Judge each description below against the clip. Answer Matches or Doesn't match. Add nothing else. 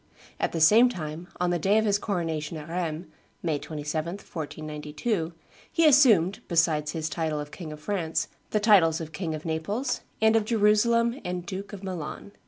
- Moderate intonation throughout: Matches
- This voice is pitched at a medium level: Matches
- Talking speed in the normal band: Matches